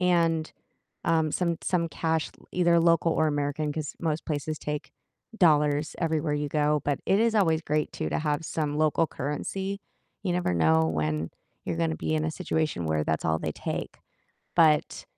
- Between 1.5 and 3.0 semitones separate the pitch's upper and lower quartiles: Yes, narrow, 2.5 semitones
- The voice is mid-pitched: Yes, medium, 155 Hz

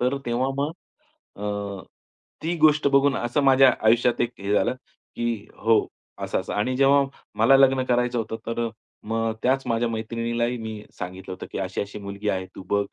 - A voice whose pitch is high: No, low, 120 Hz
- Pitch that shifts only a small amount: No, average, 3.9 semitones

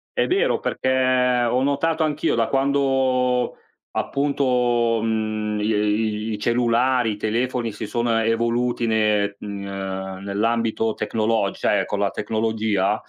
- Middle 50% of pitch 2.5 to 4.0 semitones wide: Yes, average, 2.9 semitones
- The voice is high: No, low, 115 Hz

